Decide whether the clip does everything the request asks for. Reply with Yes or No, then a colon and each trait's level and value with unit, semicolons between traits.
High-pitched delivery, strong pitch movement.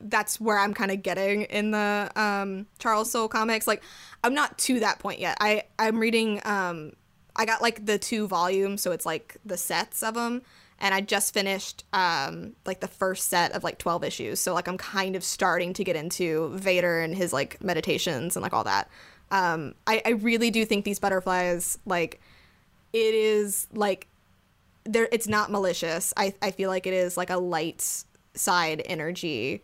No: high, 195 Hz; average, 3.2 semitones